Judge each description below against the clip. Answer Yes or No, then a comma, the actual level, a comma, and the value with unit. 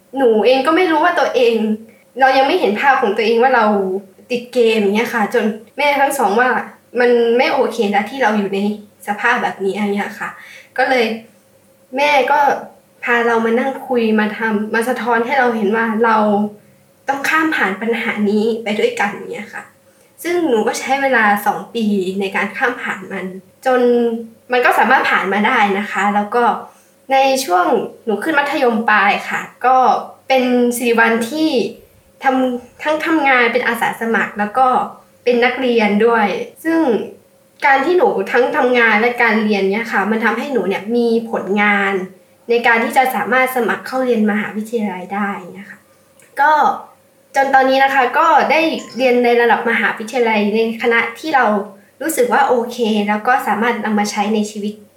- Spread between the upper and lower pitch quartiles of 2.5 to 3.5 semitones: No, average, 3.9 semitones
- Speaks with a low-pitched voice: No, high, 235 Hz